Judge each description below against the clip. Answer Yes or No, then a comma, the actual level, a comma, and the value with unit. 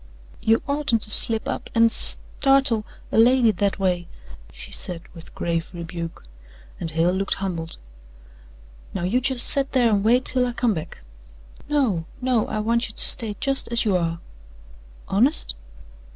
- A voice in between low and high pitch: No, high, 220 Hz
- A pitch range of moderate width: No, wide, 5.8 semitones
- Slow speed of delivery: No, average, 165 wpm